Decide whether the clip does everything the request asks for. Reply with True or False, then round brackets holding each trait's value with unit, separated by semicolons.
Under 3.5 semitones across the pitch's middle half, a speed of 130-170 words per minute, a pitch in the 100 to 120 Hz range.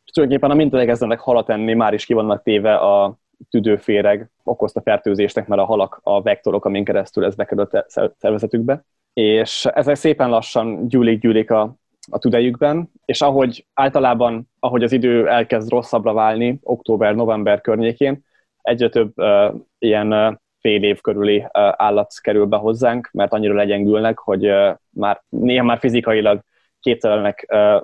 True (2.8 semitones; 150 wpm; 115 Hz)